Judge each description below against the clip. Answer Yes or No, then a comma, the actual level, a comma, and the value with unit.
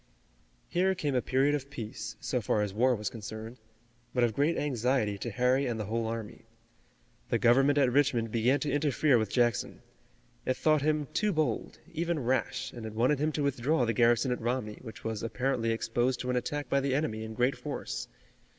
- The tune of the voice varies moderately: Yes, average, 3.8 semitones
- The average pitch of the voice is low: Yes, low, 125 Hz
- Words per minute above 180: Yes, average, 195 wpm